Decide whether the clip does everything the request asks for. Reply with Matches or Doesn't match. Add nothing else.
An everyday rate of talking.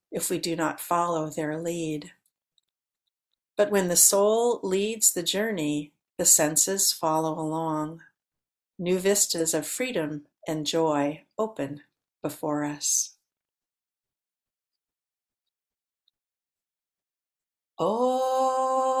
Doesn't match